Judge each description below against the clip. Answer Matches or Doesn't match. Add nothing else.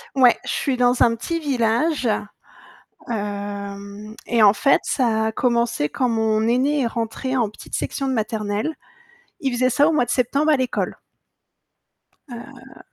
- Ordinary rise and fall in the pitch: Matches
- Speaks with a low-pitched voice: Doesn't match